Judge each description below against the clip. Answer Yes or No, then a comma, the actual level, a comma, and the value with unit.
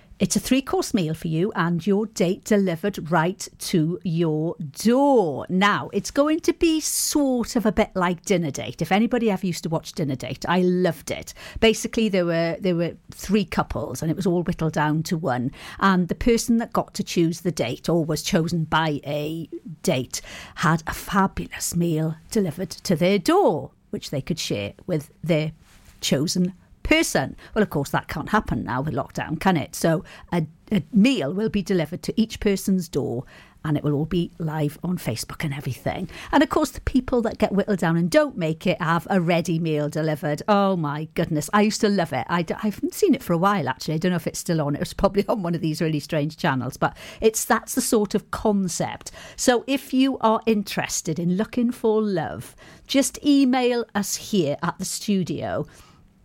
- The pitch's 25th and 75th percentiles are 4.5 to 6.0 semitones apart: Yes, average, 5.1 semitones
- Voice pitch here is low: No, medium, 180 Hz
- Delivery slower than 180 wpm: No, average, 200 wpm